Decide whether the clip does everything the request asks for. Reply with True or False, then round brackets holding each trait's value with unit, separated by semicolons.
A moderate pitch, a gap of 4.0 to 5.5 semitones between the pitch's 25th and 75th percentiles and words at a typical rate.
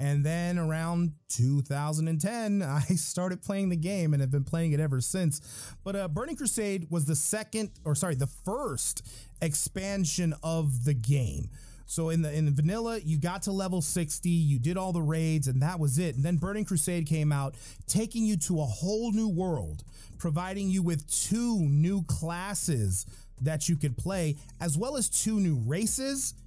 True (165 Hz; 4.6 semitones; 180 wpm)